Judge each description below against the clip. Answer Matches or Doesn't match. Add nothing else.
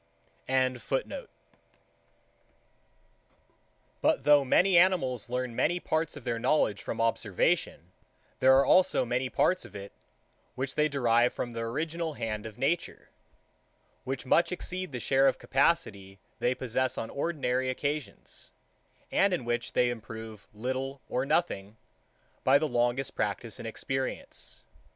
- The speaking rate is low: Matches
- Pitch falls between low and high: Doesn't match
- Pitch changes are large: Doesn't match